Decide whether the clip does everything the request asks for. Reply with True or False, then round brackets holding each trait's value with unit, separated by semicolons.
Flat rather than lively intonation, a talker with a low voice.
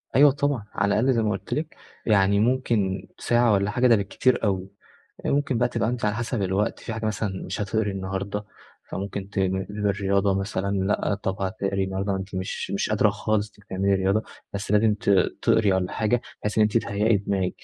True (2.3 semitones; 100 Hz)